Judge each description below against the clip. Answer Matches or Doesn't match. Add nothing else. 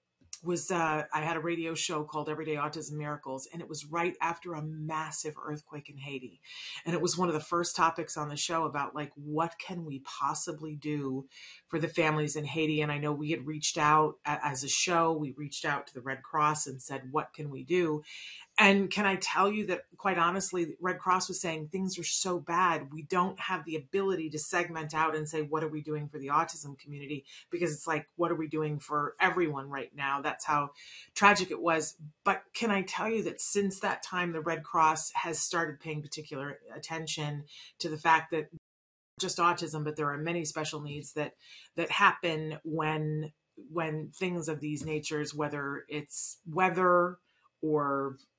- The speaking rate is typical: Matches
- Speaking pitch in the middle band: Matches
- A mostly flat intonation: Matches